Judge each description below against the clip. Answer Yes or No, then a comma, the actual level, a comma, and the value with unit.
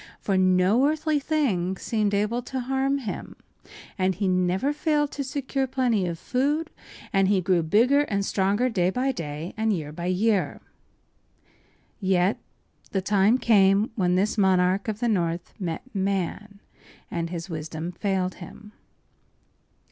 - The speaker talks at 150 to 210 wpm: No, average, 140 wpm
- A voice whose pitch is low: No, high, 200 Hz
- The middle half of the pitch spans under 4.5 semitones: No, average, 5.2 semitones